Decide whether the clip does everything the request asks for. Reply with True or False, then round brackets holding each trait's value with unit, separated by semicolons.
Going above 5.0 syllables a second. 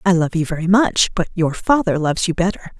True (6.0 syllables/s)